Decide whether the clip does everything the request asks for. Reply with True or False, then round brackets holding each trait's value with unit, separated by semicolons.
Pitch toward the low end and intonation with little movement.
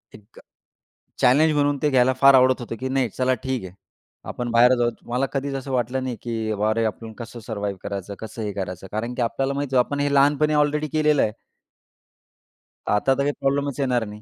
False (125 Hz; 3.6 semitones)